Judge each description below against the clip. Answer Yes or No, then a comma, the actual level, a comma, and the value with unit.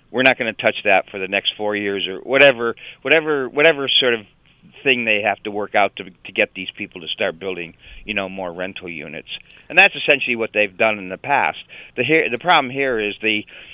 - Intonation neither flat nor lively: No, wide, 6.2 semitones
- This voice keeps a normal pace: No, fast, 225 wpm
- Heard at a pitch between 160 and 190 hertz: No, low, 110 Hz